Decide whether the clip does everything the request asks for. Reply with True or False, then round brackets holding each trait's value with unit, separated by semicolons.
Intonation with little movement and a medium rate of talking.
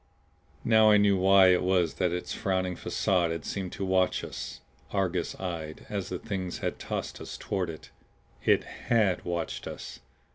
True (1.9 semitones; 170 wpm)